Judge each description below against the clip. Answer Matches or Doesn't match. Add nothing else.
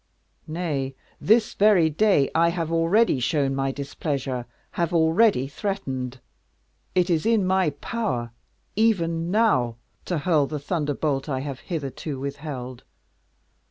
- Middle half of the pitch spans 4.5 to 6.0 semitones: Matches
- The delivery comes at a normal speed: Doesn't match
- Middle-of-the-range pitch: Matches